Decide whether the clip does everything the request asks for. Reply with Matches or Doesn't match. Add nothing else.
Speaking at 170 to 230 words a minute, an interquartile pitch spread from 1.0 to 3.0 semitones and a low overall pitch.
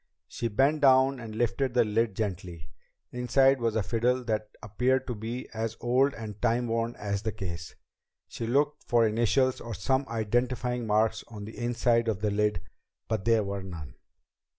Matches